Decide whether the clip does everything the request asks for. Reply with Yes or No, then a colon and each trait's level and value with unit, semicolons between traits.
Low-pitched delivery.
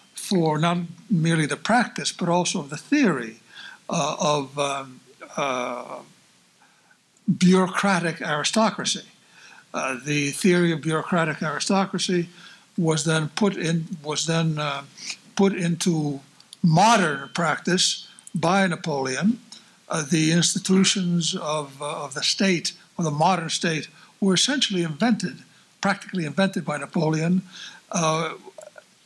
No: medium, 175 Hz